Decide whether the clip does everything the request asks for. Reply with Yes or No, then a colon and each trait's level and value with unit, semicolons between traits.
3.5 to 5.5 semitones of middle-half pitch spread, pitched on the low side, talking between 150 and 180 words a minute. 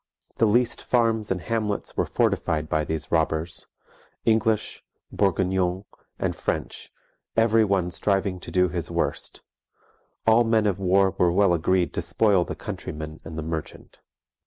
No: average, 4.0 semitones; very low, 95 Hz; average, 140 wpm